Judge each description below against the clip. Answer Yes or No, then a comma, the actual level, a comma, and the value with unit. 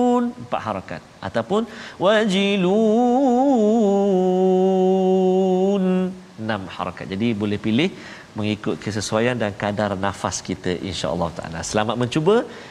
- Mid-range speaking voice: No, low, 125 Hz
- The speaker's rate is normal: Yes, average, 90 wpm